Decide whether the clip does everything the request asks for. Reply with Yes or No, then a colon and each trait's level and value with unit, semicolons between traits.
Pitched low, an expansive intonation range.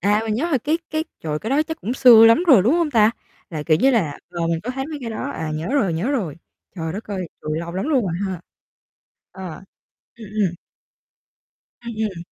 No: high, 215 Hz; wide, 7.3 semitones